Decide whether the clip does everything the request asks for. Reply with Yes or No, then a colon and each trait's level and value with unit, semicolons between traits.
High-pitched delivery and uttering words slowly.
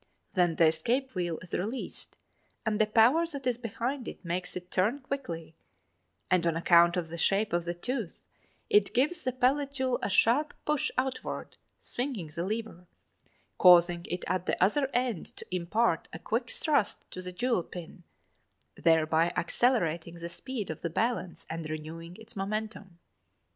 No: high, 195 Hz; average, 165 wpm